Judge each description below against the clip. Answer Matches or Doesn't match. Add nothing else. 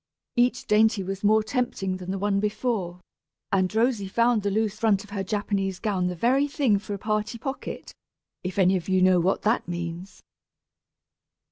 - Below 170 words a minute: Doesn't match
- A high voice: Matches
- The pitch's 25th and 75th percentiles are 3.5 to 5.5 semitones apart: Doesn't match